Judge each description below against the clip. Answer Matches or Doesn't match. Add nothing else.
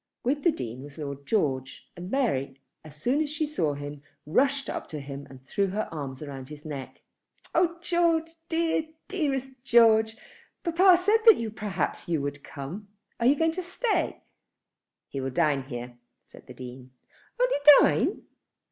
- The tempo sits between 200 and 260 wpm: Doesn't match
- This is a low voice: Doesn't match